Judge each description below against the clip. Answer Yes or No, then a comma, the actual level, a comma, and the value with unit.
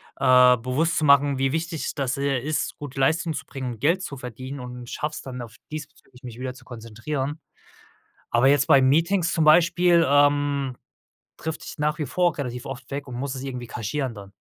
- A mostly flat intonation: No, average, 3.2 semitones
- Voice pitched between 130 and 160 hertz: Yes, medium, 140 Hz